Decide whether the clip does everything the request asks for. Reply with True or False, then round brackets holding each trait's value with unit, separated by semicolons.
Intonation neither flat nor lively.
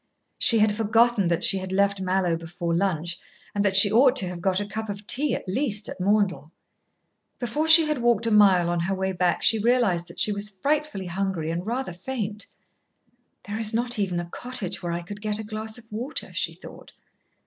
True (3.8 semitones)